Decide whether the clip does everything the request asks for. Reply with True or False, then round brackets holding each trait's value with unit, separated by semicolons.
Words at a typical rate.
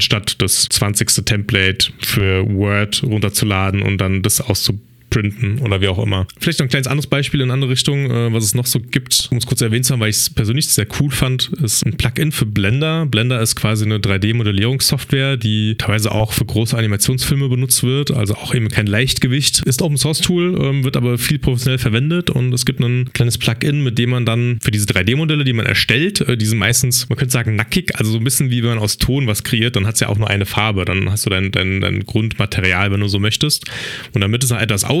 False (230 wpm)